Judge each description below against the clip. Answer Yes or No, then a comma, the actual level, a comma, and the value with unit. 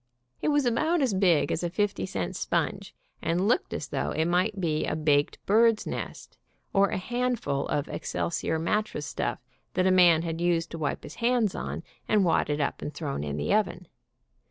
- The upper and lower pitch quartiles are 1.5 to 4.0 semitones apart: No, wide, 5.4 semitones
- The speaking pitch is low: No, medium, 180 Hz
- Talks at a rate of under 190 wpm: No, average, 200 wpm